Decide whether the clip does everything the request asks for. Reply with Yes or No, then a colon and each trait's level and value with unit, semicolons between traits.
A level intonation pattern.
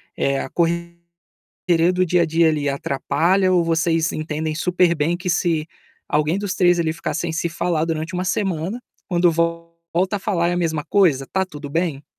Yes: narrow, 2.1 semitones